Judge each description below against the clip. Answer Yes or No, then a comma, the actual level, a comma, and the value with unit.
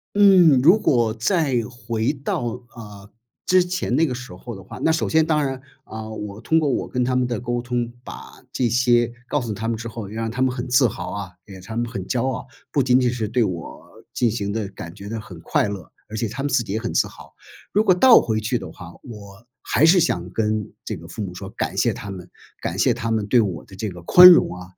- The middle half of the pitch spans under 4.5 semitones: Yes, average, 4.0 semitones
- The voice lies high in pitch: No, low, 115 Hz